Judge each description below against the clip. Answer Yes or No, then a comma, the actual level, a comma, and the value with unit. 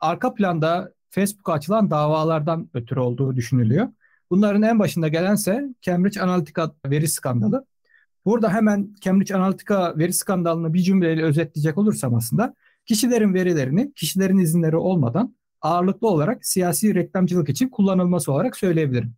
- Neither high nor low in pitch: Yes, medium, 180 Hz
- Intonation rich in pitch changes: No, average, 4.4 semitones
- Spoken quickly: No, average, 125 wpm